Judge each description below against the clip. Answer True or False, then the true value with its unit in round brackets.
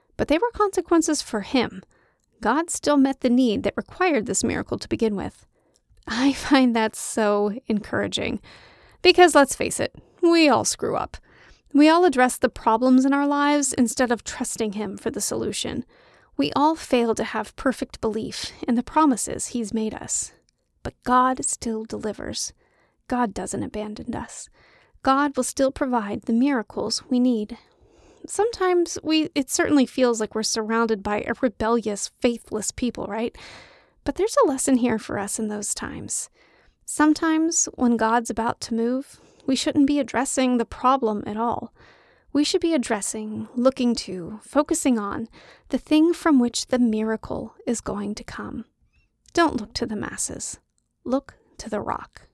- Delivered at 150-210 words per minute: True (160 wpm)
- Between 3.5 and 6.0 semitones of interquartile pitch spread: True (4.5 semitones)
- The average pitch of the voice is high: True (250 Hz)